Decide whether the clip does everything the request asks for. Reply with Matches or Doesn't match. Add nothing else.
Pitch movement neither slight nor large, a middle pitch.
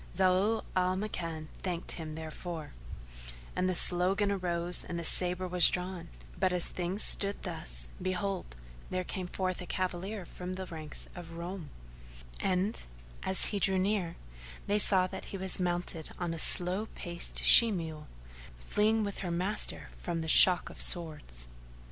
Doesn't match